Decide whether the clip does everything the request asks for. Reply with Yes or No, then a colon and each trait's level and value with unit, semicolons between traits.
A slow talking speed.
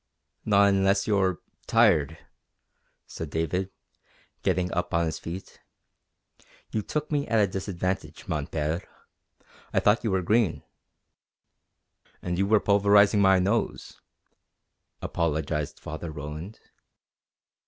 Yes: slow, 110 wpm